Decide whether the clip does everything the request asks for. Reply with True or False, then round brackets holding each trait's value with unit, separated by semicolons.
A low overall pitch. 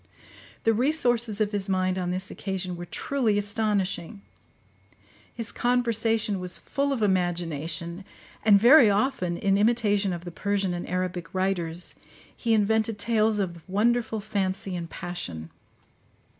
False (200 Hz)